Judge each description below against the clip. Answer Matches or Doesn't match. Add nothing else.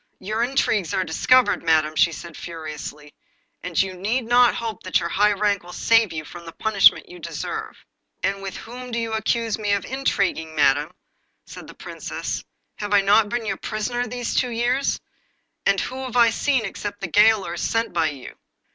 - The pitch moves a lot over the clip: Doesn't match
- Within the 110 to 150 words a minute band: Doesn't match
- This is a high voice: Matches